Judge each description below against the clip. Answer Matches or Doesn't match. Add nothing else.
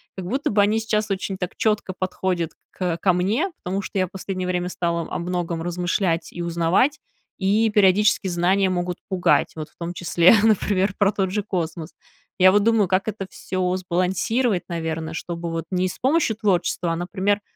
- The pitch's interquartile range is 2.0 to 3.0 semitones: Matches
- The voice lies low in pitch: Doesn't match